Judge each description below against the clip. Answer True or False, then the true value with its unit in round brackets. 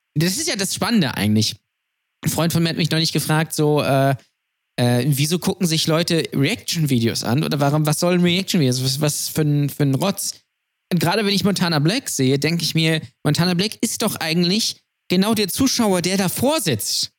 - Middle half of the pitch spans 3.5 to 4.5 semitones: True (4.1 semitones)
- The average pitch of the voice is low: False (160 Hz)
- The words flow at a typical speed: False (200 wpm)